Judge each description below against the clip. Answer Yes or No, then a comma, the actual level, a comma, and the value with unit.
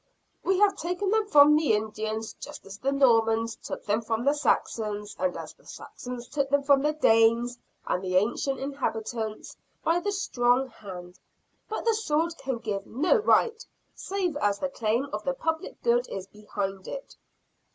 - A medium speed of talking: Yes, average, 170 wpm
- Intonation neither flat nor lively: No, wide, 6.2 semitones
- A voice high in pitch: Yes, very high, 250 Hz